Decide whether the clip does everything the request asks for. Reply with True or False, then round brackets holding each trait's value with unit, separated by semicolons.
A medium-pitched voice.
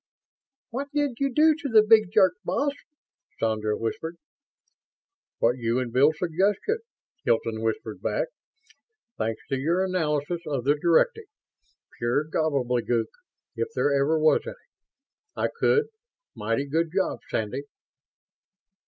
True (155 Hz)